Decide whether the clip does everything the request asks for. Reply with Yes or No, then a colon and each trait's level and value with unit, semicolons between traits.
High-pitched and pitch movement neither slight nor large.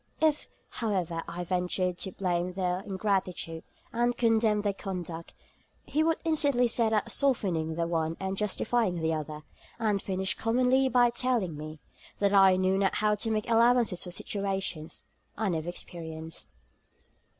Yes: high, 195 Hz; average, 4.6 semitones